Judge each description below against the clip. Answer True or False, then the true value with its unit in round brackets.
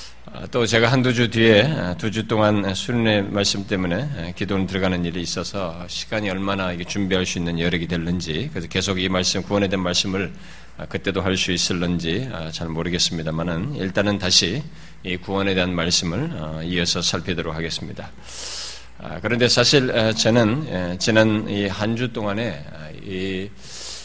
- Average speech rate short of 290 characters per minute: False (315 characters per minute)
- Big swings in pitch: False (3.3 semitones)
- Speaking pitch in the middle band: False (95 Hz)